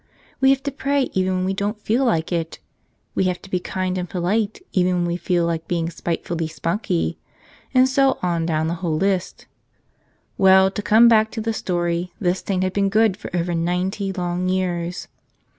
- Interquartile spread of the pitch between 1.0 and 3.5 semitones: Yes, average, 3.1 semitones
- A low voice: No, medium, 185 Hz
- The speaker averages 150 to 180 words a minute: No, average, 195 wpm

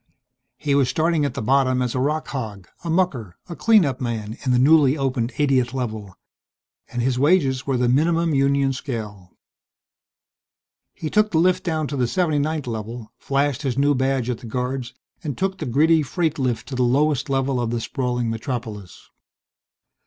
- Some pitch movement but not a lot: Yes, average, 3.8 semitones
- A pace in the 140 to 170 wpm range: No, average, 180 wpm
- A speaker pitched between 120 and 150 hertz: Yes, low, 135 Hz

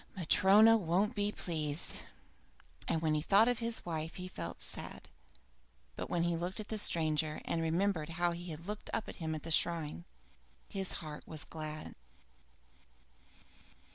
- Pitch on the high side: No, medium, 170 Hz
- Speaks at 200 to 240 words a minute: No, average, 160 wpm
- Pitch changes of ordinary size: Yes, average, 3.9 semitones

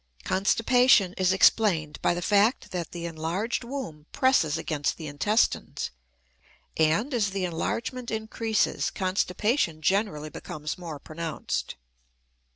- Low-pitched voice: No, medium, 185 Hz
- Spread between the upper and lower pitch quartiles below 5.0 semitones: No, wide, 5.5 semitones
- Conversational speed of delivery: No, slow, 115 wpm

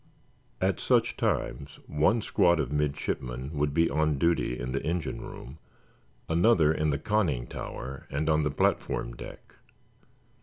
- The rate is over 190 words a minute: No, average, 145 wpm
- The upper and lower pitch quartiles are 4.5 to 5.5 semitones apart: No, average, 3.4 semitones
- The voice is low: Yes, very low, 75 Hz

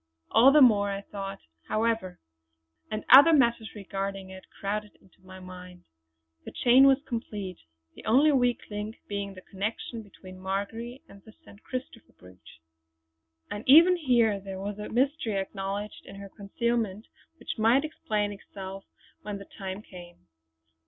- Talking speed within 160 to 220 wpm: No, average, 150 wpm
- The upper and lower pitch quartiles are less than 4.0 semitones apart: Yes, average, 3.3 semitones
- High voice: Yes, high, 205 Hz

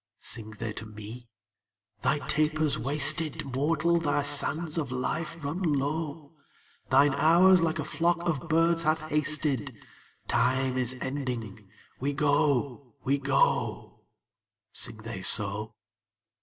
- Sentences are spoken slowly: Yes, slow, 120 wpm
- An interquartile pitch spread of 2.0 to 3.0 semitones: No, average, 3.7 semitones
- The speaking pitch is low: No, medium, 145 Hz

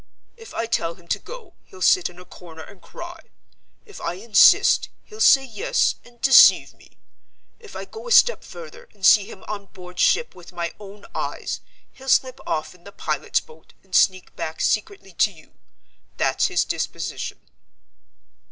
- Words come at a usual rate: Yes, average, 175 wpm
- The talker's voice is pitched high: Yes, high, 205 Hz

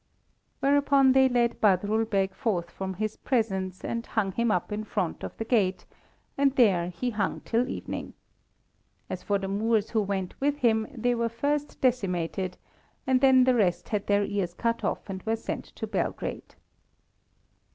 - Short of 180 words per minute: Yes, average, 170 wpm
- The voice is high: Yes, high, 220 Hz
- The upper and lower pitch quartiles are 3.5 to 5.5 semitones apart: Yes, average, 4.2 semitones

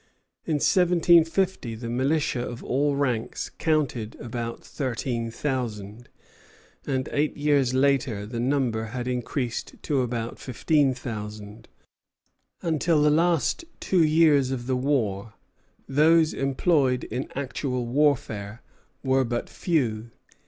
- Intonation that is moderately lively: Yes, average, 4.0 semitones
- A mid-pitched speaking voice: No, low, 130 Hz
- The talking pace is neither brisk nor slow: No, slow, 115 wpm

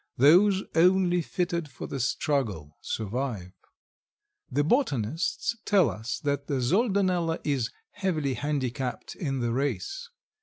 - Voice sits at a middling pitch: Yes, medium, 145 Hz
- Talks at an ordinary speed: No, slow, 115 wpm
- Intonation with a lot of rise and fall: Yes, wide, 6.1 semitones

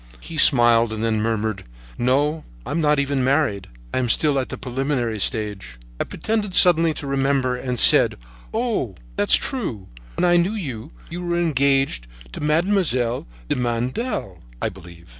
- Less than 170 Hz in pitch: Yes, low, 135 Hz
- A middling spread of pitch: No, wide, 5.9 semitones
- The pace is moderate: Yes, average, 160 wpm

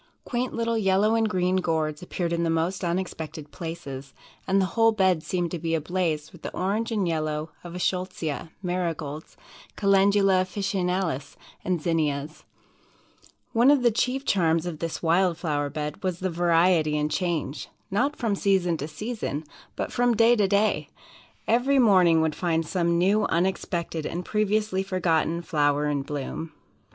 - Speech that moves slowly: No, average, 160 wpm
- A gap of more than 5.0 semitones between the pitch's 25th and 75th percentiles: No, average, 3.6 semitones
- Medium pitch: Yes, medium, 175 Hz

